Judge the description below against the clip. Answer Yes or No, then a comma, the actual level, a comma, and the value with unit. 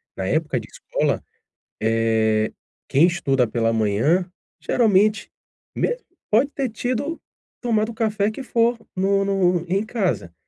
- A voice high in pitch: Yes, high, 195 Hz